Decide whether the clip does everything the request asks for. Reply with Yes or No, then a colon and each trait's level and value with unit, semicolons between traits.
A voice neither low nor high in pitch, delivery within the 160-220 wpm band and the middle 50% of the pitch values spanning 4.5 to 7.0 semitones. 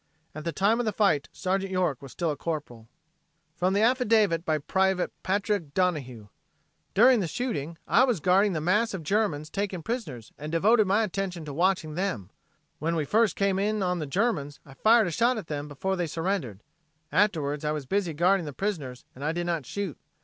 Yes: medium, 180 Hz; average, 195 wpm; average, 5.1 semitones